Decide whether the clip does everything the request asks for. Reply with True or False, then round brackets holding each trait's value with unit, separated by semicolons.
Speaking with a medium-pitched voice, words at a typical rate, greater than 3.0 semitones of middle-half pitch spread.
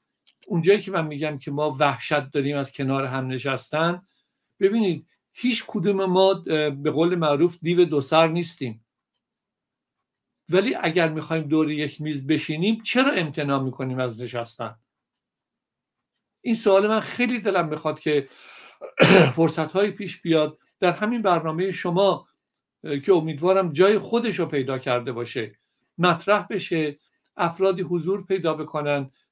True (165 Hz; 130 wpm; 4.7 semitones)